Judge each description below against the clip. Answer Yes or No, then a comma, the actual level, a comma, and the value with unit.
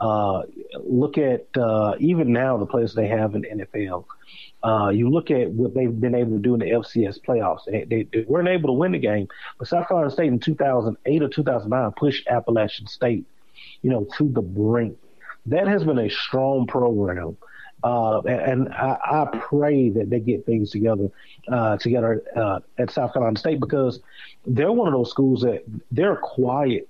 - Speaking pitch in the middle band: No, low, 120 Hz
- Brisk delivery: No, average, 190 wpm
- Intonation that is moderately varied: Yes, average, 3.5 semitones